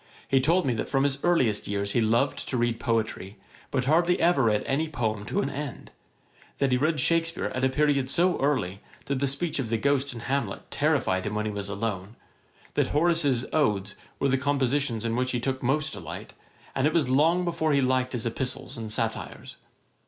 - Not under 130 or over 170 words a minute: No, fast, 205 wpm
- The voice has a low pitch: Yes, low, 130 Hz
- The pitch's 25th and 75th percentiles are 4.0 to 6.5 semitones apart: Yes, average, 4.4 semitones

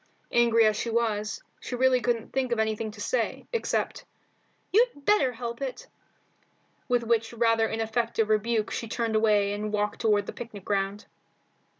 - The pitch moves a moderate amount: No, narrow, 2.0 semitones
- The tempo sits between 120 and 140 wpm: No, average, 160 wpm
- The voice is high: Yes, high, 225 Hz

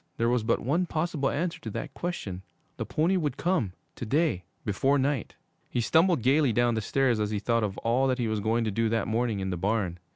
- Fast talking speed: Yes, fast, 230 wpm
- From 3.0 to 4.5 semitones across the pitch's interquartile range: No, average, 5.1 semitones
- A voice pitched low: Yes, low, 120 Hz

